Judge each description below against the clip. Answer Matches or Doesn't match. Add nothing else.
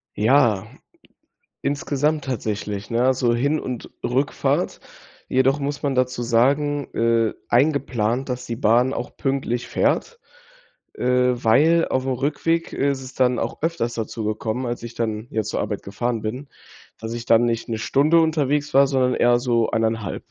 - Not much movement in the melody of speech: Doesn't match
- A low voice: Matches